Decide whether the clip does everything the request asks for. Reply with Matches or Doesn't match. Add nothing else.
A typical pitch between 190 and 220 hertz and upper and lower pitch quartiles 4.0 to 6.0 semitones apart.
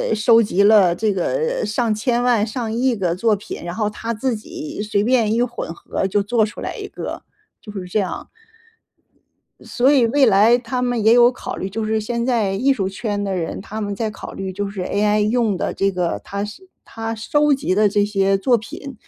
Doesn't match